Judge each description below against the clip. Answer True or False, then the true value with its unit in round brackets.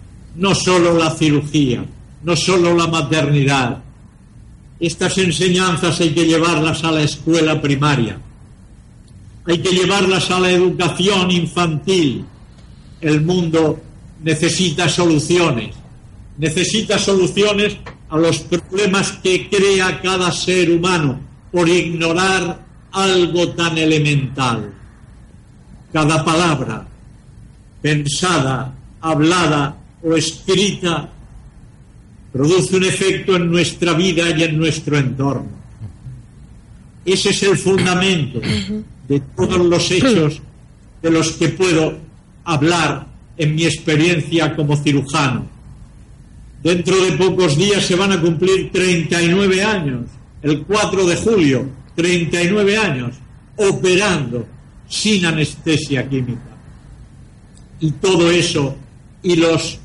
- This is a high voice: False (165 Hz)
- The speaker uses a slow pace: True (100 wpm)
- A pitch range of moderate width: True (4.8 semitones)